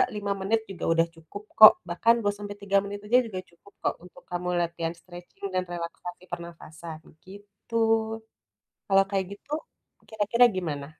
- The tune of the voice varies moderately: Yes, average, 3.0 semitones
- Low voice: No, medium, 185 Hz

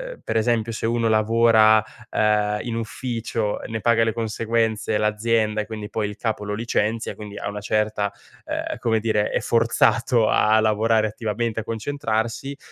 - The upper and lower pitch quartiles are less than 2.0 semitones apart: Yes, narrow, 1.3 semitones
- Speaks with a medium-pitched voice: No, low, 110 Hz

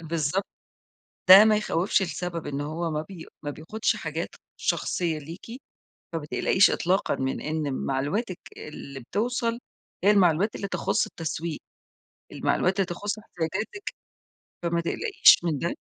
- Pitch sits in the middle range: Yes, medium, 170 Hz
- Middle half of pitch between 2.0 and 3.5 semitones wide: No, average, 4.5 semitones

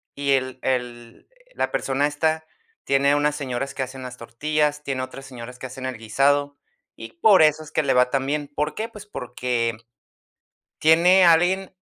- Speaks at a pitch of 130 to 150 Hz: Yes, medium, 140 Hz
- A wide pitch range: No, average, 3.1 semitones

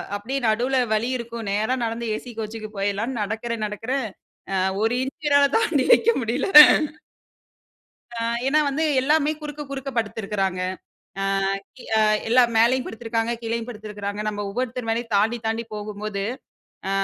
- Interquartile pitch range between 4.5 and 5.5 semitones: No, average, 3.2 semitones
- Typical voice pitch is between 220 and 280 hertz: Yes, high, 230 Hz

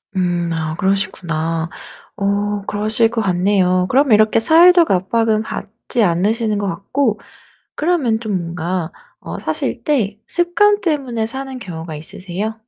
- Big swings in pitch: No, average, 4.8 semitones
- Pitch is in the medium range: No, high, 210 Hz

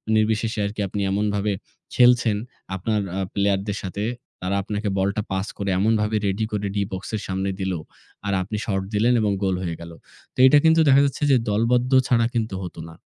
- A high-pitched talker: No, low, 105 Hz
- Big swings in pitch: No, narrow, 2.5 semitones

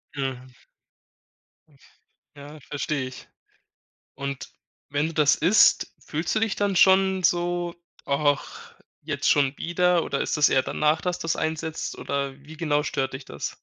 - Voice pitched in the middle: Yes, medium, 150 Hz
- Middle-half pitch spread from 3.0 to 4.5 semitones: Yes, average, 3.7 semitones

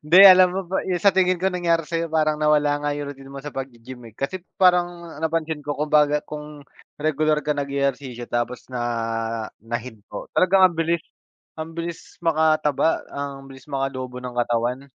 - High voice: No, medium, 150 Hz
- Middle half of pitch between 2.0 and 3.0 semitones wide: No, average, 4.0 semitones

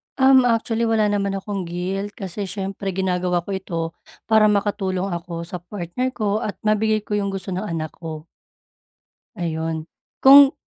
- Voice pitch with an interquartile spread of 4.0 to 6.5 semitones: No, average, 3.2 semitones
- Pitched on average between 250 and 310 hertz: No, high, 195 Hz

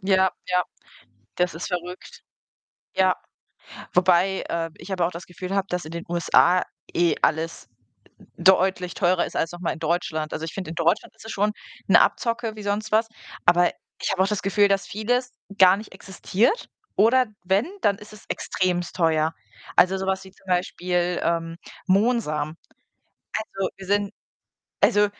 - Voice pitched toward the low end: No, medium, 185 Hz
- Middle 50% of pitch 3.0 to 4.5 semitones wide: No, narrow, 2.5 semitones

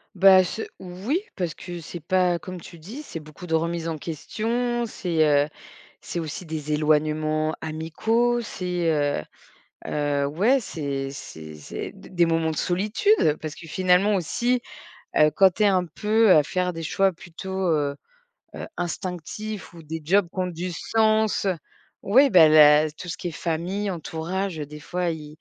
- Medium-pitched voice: Yes, medium, 170 Hz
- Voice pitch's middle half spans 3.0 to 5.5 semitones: Yes, average, 3.8 semitones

